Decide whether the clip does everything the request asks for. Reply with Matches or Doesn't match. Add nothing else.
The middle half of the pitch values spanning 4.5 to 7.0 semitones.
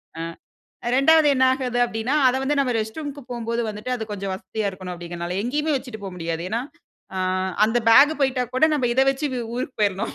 Matches